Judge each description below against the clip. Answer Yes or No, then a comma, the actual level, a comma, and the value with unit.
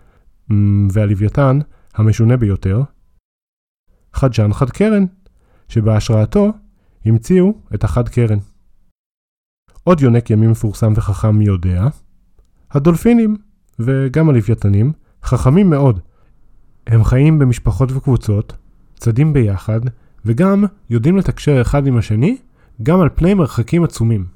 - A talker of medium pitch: No, low, 120 Hz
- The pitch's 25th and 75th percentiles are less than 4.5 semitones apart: No, average, 5.2 semitones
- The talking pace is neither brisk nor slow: No, slow, 95 wpm